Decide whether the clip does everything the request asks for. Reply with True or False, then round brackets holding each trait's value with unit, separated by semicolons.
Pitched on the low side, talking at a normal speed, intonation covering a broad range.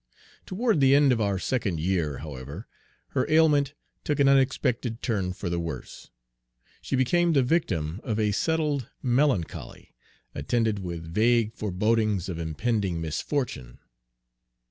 False (110 Hz; 130 wpm; 7.8 semitones)